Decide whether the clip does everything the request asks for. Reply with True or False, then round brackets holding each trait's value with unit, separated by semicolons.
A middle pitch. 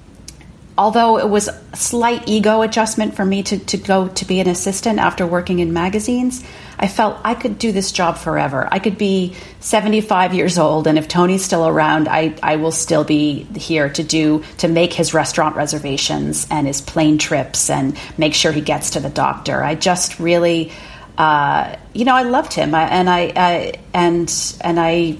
True (175 Hz)